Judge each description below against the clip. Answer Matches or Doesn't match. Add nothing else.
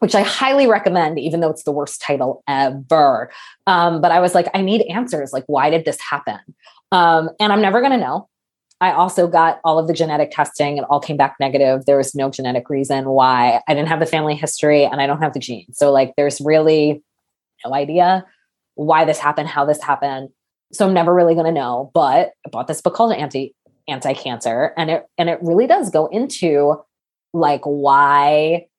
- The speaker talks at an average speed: Doesn't match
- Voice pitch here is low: Doesn't match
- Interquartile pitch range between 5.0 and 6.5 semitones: Doesn't match